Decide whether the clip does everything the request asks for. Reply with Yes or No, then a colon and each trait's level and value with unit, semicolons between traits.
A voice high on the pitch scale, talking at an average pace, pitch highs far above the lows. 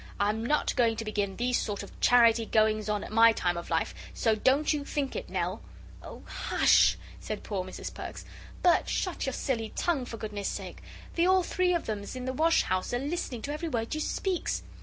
No: high, 235 Hz; fast, 210 wpm; wide, 5.7 semitones